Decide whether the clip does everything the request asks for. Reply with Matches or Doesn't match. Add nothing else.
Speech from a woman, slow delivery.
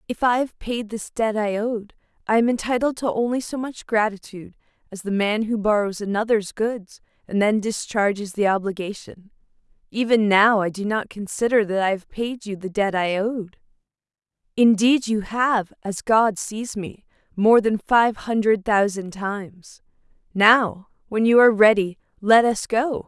Doesn't match